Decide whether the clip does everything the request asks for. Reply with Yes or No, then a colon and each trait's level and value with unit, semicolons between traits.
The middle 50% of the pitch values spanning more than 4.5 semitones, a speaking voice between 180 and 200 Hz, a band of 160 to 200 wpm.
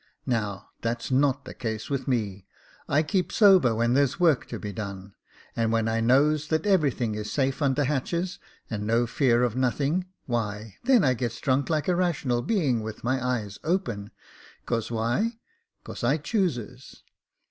No: average, 5.1 semitones; low, 125 Hz; average, 175 wpm